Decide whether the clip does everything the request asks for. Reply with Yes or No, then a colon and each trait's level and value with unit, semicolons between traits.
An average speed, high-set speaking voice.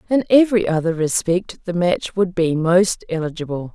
No: average, 160 wpm; medium, 180 Hz